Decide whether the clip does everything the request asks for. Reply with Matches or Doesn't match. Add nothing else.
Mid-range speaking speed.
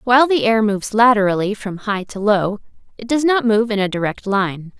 Doesn't match